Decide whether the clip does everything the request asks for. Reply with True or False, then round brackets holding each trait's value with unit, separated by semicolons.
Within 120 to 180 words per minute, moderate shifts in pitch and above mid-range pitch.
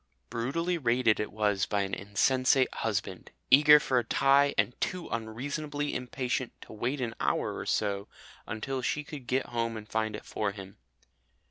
False (165 wpm; 4.3 semitones; 120 Hz)